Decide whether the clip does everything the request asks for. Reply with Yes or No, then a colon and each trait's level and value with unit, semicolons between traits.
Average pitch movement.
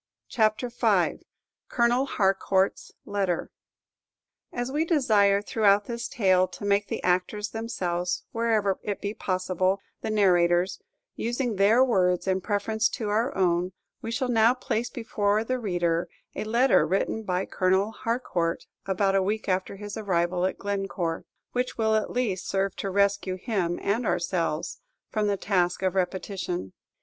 Yes: average, 3.3 semitones